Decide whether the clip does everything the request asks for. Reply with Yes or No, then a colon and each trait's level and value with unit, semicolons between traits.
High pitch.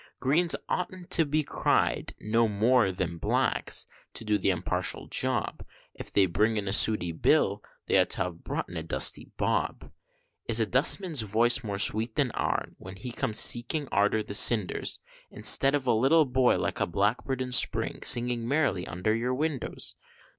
No: low, 115 Hz